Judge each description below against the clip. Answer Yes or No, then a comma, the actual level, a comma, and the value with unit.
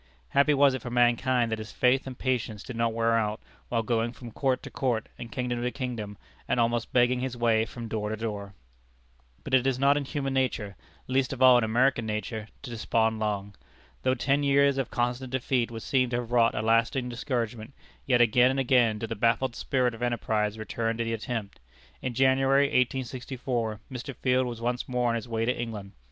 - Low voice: Yes, low, 120 Hz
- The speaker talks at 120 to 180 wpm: No, fast, 205 wpm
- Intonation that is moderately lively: No, narrow, 2.3 semitones